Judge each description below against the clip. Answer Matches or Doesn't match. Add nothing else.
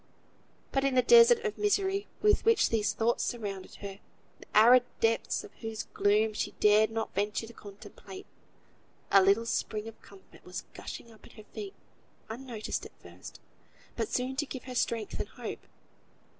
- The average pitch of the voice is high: Matches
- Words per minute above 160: Matches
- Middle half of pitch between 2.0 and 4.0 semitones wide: Doesn't match